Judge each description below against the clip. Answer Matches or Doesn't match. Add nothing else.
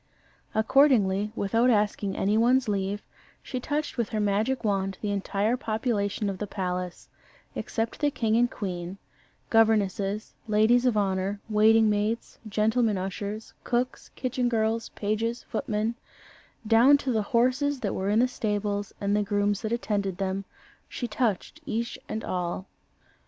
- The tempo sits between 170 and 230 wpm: Doesn't match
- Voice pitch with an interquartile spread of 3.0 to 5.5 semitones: Doesn't match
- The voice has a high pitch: Matches